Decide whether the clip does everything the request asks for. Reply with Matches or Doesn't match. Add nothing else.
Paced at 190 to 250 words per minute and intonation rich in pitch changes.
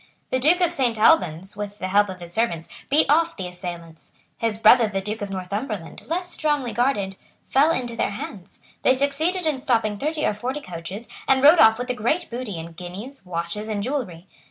Matches